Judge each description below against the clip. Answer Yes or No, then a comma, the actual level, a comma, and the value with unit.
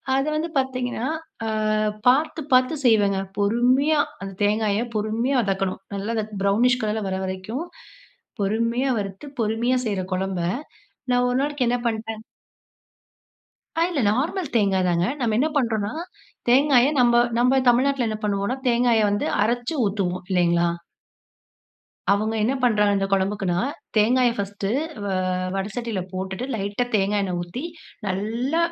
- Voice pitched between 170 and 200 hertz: No, high, 220 Hz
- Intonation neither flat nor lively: Yes, average, 4.0 semitones